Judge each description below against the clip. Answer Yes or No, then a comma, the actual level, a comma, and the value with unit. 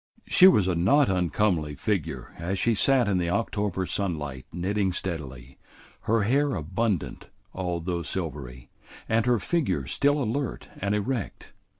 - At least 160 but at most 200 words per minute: No, slow, 135 wpm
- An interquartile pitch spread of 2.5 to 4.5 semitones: No, average, 5.2 semitones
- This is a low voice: Yes, very low, 95 Hz